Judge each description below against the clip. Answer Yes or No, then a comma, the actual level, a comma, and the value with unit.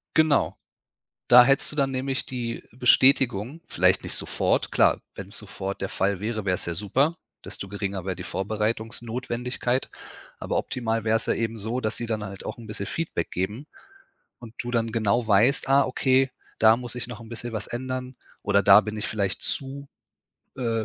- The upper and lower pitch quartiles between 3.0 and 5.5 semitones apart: Yes, average, 3.6 semitones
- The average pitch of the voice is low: Yes, low, 115 Hz